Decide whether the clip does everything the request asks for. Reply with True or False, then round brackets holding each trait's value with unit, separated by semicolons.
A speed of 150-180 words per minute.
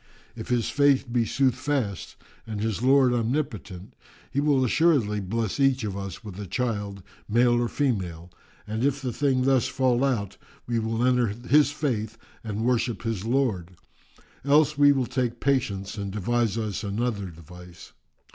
True (155 wpm)